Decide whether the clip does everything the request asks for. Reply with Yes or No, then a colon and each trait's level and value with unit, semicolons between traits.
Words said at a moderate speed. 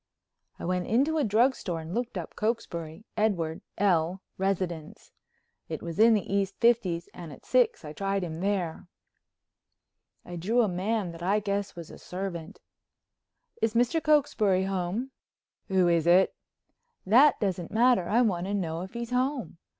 Yes: average, 155 wpm